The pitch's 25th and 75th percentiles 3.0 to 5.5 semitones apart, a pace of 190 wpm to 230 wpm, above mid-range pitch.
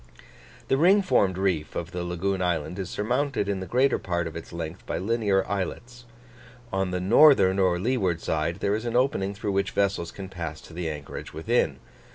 No: average, 4.1 semitones; average, 195 wpm; very low, 95 Hz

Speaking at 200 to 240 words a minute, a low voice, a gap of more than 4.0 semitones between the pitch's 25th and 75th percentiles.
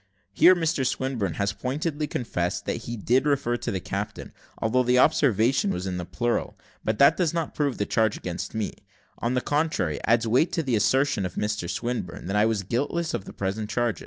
Yes: fast, 205 wpm; low, 115 Hz; average, 5.2 semitones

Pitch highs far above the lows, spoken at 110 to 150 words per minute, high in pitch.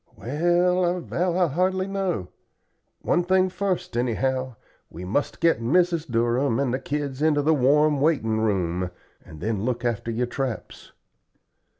No: wide, 6.7 semitones; average, 145 wpm; medium, 140 Hz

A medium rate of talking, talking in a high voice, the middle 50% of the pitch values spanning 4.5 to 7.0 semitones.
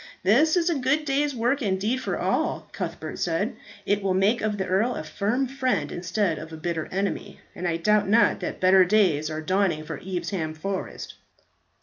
Yes: average, 190 wpm; high, 195 Hz; average, 5.2 semitones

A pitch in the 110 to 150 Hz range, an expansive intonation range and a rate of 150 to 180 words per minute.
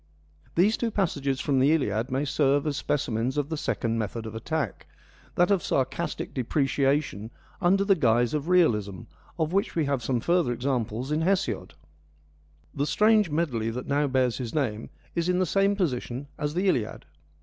Yes: medium, 140 Hz; wide, 5.7 semitones; average, 170 wpm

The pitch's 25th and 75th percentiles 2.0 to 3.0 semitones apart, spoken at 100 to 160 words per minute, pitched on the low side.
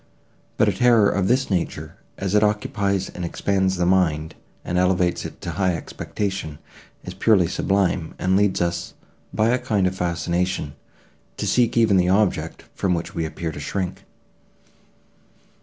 Yes: narrow, 2.6 semitones; average, 155 wpm; very low, 95 Hz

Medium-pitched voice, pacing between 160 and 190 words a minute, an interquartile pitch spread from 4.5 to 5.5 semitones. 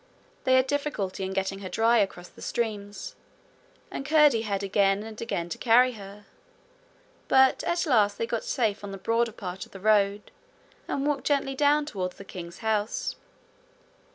No: high, 215 Hz; average, 170 wpm; average, 5.0 semitones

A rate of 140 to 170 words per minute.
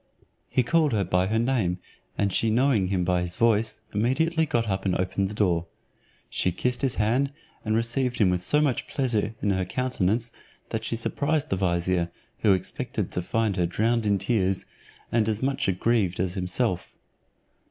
No: average, 180 wpm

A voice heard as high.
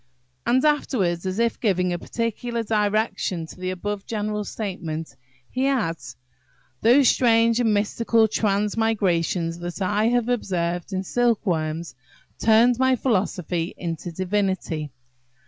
Yes: high, 205 Hz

